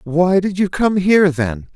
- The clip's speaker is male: Yes, male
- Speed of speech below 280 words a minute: Yes, fast, 205 wpm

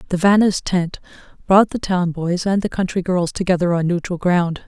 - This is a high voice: No, medium, 180 Hz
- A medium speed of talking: Yes, average, 195 wpm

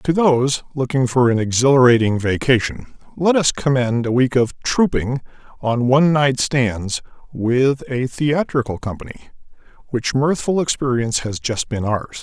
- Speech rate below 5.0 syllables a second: Yes, 4.7 syllables/s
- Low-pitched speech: Yes, low, 130 Hz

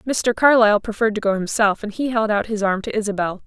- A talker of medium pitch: No, high, 215 Hz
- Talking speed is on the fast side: Yes, fast, 245 wpm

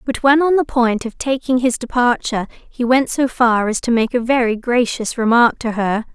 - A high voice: Yes, high, 240 Hz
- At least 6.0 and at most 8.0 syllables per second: No, 4.9 syllables/s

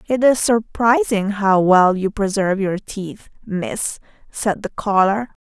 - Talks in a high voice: Yes, high, 205 Hz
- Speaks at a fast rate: No, average, 145 wpm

